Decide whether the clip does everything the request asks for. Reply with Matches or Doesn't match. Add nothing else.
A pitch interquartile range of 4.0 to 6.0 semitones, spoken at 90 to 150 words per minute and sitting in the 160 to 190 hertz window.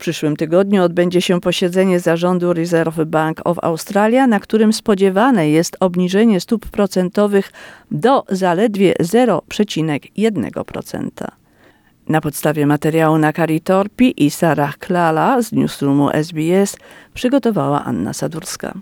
Matches